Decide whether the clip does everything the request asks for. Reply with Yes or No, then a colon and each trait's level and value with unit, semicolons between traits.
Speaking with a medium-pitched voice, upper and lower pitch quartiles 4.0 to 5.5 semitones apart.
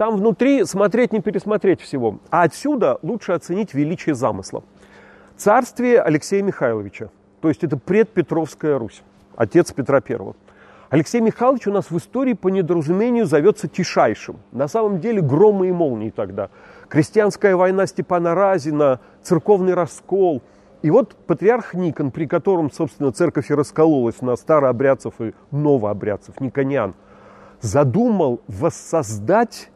No: medium, 170 Hz; wide, 6.6 semitones